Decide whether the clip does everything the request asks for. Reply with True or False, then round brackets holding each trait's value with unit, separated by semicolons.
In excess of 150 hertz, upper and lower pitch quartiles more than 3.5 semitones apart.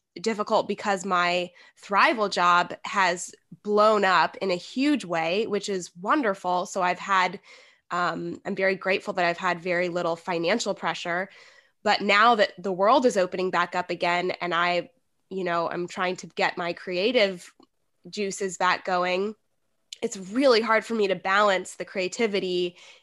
False (185 Hz; 2.4 semitones)